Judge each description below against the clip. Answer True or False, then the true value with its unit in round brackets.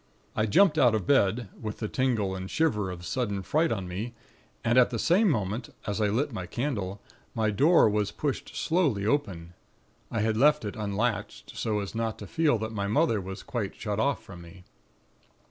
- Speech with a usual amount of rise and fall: True (4.0 semitones)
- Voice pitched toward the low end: True (110 Hz)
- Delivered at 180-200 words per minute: True (195 wpm)